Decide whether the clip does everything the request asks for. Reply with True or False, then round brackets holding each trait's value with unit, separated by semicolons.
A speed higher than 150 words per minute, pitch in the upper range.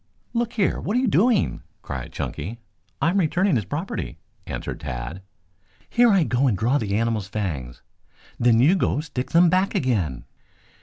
False (165 wpm; 130 Hz)